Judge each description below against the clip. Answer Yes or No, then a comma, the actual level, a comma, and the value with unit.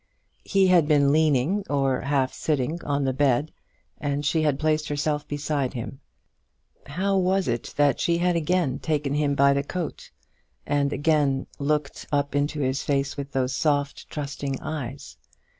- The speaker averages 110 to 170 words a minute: Yes, average, 160 wpm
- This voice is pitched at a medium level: Yes, medium, 145 Hz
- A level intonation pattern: Yes, narrow, 2.0 semitones